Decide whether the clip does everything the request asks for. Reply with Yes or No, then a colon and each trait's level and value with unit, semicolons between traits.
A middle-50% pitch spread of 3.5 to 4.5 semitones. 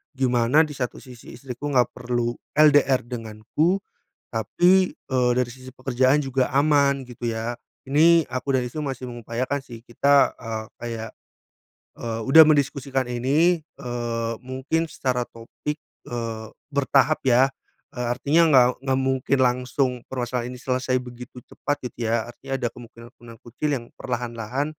No: average, 2.7 semitones